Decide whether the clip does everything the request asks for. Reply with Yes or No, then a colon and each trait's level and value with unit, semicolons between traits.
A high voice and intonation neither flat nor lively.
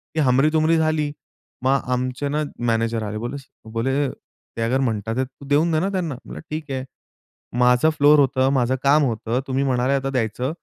No: low, 135 Hz; average, 3.3 semitones